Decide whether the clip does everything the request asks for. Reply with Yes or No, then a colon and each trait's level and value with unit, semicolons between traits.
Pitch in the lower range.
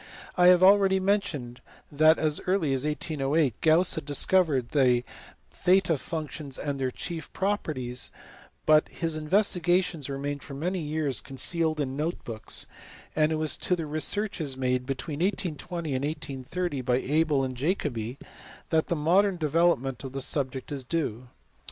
No: medium, 150 Hz